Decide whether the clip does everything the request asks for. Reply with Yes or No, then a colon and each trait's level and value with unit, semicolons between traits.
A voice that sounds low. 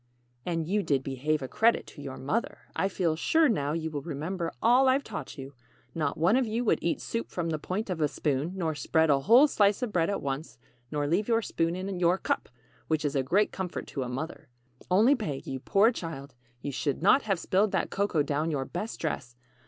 No: medium, 165 Hz